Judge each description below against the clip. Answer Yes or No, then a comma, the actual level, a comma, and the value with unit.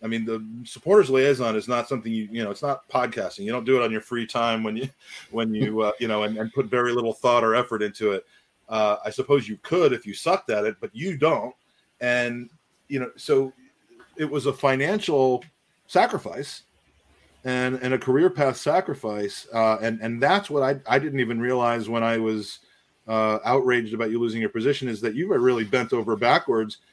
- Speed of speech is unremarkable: No, fast, 210 wpm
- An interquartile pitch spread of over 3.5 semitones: No, average, 3.0 semitones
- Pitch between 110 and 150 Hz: Yes, low, 120 Hz